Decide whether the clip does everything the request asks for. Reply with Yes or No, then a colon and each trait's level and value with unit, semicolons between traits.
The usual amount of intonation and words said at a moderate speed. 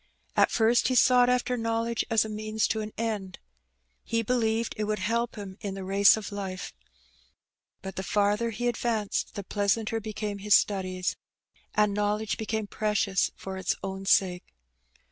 No: narrow, 2.3 semitones; average, 165 wpm